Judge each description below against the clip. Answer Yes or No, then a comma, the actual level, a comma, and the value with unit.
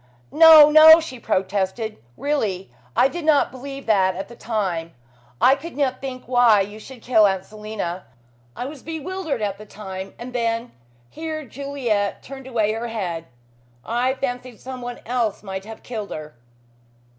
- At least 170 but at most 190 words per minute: No, average, 160 wpm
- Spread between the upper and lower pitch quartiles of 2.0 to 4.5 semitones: No, average, 5.0 semitones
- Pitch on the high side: Yes, high, 235 Hz